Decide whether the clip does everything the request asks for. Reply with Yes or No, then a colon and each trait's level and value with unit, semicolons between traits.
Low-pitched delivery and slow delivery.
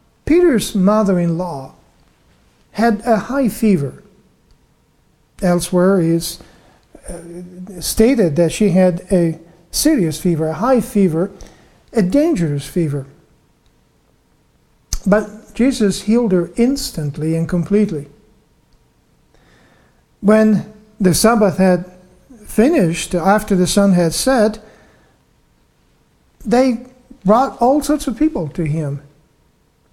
No: high, 195 Hz; slow, 90 wpm